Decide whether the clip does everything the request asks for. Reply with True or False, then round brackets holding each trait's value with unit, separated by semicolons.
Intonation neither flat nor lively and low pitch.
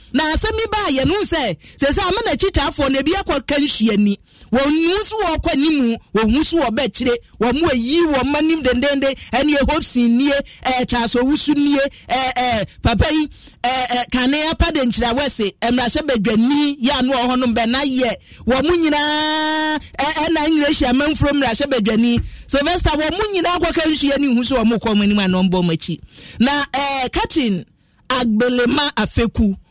False (4.0 semitones; 275 Hz)